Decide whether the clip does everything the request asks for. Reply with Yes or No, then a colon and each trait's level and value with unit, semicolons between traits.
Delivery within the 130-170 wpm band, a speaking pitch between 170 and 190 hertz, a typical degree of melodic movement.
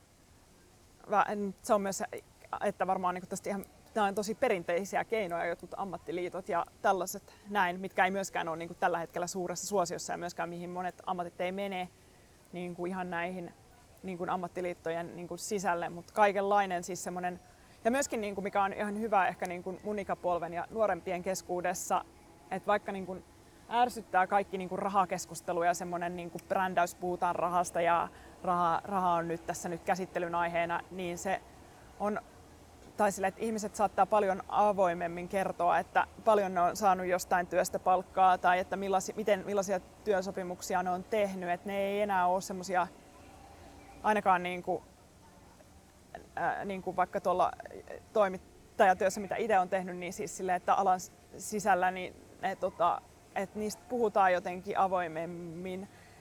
No: average, 135 wpm; medium, 185 Hz; narrow, 2.2 semitones